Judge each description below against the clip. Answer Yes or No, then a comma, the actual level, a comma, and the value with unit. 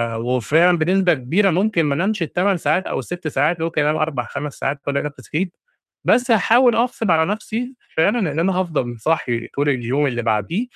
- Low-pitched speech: No, medium, 160 Hz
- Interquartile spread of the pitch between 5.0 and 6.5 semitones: Yes, wide, 5.4 semitones